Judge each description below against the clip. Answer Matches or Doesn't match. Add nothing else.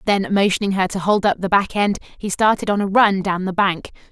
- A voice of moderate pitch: Doesn't match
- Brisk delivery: Matches